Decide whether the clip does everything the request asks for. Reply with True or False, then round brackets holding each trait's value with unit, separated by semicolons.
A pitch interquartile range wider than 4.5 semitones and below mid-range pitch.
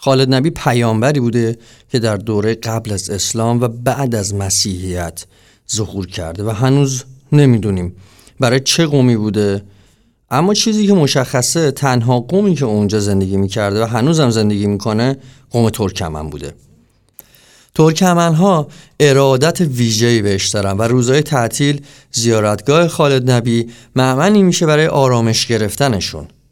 True (4.9 semitones; 120 Hz)